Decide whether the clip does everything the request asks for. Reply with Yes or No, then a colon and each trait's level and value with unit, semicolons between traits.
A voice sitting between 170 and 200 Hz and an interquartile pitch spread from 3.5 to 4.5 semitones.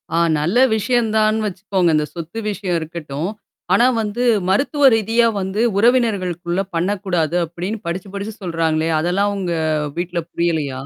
Yes: high, 190 Hz; average, 4.0 semitones